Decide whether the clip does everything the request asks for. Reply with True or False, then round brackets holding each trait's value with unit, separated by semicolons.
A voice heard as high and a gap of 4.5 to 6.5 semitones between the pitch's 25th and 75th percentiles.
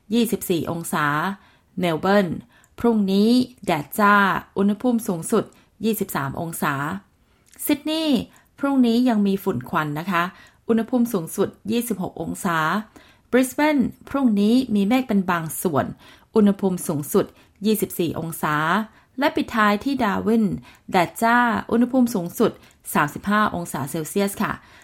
True (205 Hz; 4.8 semitones)